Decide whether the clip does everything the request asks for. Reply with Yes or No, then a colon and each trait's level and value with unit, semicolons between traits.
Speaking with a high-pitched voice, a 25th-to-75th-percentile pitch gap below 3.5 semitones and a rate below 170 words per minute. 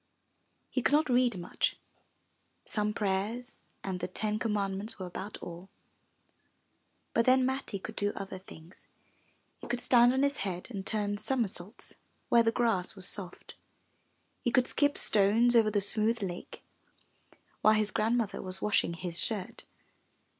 No: high, 210 Hz; average, 3.8 semitones; average, 155 wpm